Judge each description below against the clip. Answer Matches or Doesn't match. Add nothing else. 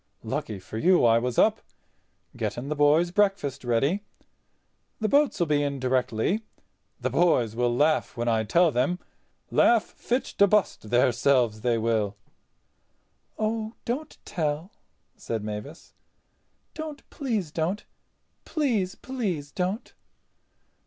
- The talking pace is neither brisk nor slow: Doesn't match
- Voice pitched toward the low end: Doesn't match